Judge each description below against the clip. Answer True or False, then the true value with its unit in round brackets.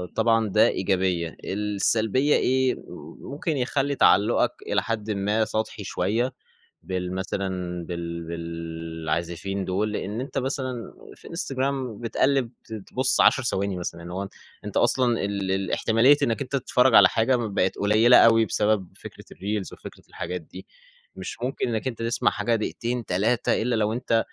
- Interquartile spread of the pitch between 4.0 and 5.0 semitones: True (4.4 semitones)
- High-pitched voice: False (110 Hz)